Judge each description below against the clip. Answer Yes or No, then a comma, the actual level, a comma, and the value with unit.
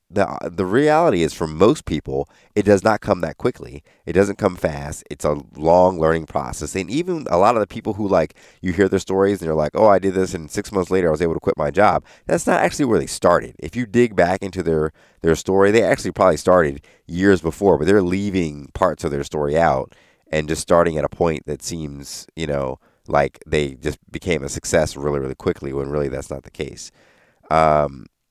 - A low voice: Yes, very low, 80 Hz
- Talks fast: Yes, fast, 225 wpm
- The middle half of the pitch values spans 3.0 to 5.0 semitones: Yes, average, 4.4 semitones